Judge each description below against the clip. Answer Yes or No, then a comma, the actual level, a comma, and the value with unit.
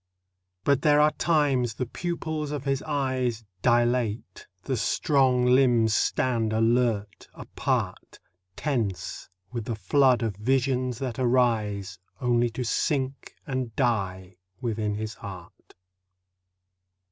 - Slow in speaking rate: Yes, slow, 110 wpm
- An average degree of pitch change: Yes, average, 3.4 semitones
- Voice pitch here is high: No, low, 125 Hz